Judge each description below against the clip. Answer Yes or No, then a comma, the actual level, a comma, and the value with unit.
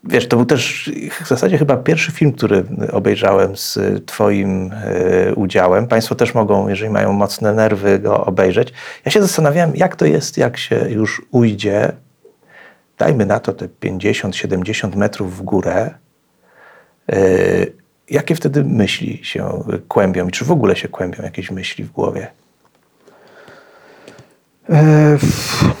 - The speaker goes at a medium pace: Yes, average, 135 wpm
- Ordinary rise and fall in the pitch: No, wide, 6.8 semitones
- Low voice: Yes, low, 120 Hz